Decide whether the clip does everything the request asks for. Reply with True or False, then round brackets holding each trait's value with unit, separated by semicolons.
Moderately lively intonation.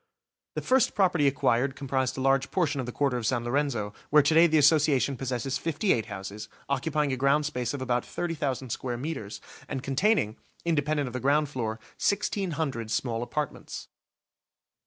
True (3.5 semitones)